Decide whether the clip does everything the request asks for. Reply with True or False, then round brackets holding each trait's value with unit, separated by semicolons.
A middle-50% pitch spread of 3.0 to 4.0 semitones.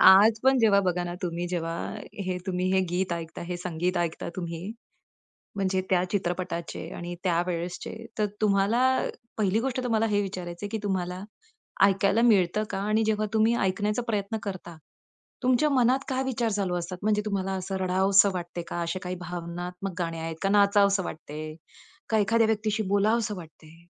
True (3.3 semitones)